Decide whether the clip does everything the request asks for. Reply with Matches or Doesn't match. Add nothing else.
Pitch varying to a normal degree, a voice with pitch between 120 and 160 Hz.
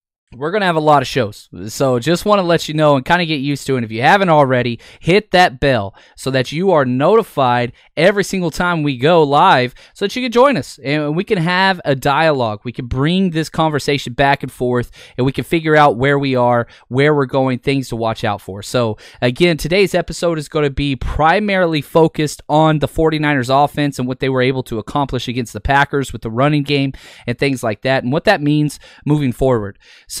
Matches